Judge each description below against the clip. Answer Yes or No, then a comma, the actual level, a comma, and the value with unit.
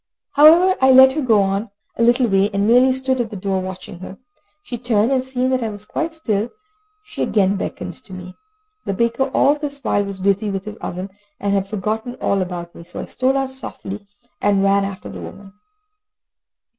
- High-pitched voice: Yes, high, 210 Hz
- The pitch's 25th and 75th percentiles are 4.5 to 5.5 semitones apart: Yes, average, 5.0 semitones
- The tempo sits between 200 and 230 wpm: Yes, fast, 205 wpm